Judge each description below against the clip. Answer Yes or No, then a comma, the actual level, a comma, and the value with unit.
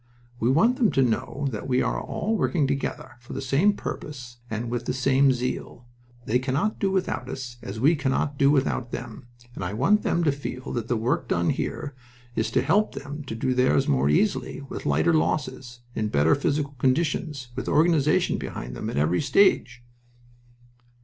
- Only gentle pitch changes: No, average, 3.5 semitones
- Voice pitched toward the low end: Yes, low, 130 Hz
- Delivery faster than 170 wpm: Yes, average, 185 wpm